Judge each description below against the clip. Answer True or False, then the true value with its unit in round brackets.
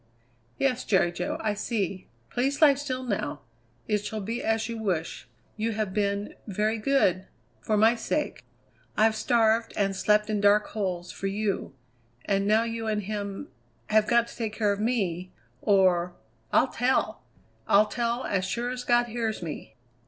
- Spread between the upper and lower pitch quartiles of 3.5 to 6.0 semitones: False (2.8 semitones)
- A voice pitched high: True (215 Hz)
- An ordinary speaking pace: True (165 wpm)